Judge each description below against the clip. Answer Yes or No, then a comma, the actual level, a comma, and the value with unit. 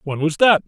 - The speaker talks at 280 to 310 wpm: No, fast, 265 wpm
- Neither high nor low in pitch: Yes, medium, 165 Hz